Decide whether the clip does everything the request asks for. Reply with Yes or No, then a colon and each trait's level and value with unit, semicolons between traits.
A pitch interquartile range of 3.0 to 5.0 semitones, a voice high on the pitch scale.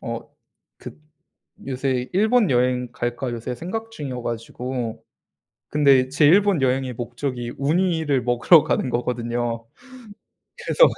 No: average, 3.7 semitones; low, 130 Hz